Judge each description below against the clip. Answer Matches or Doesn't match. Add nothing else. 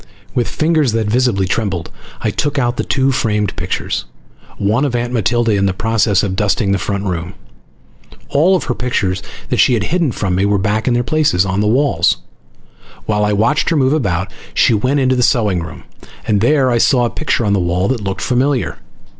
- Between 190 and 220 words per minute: Matches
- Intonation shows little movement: Doesn't match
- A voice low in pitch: Matches